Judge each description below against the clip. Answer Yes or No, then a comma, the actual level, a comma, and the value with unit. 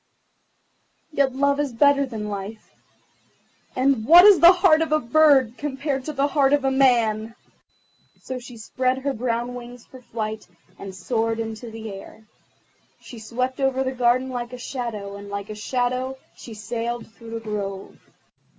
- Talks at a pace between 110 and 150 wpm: No, average, 165 wpm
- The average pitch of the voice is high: Yes, high, 245 Hz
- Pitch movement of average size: Yes, average, 3.2 semitones